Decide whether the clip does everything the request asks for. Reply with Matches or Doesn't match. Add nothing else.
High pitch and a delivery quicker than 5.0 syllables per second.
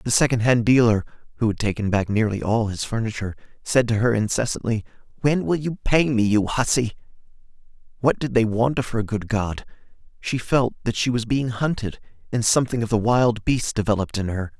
Doesn't match